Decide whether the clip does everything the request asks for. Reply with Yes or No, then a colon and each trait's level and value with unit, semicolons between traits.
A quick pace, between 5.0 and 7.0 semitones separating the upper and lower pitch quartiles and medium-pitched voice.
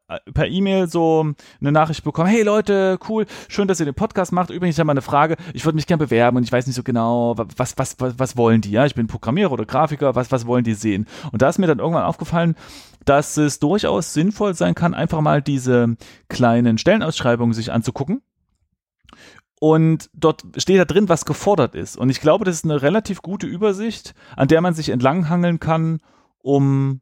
Yes: fast, 210 wpm; average, 5.3 semitones; medium, 150 Hz